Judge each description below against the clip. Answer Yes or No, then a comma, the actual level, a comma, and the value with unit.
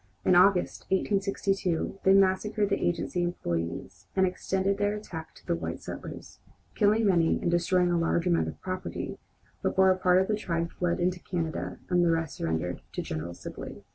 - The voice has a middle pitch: Yes, medium, 180 Hz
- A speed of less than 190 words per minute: Yes, average, 175 wpm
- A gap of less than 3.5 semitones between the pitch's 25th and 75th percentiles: Yes, narrow, 2.6 semitones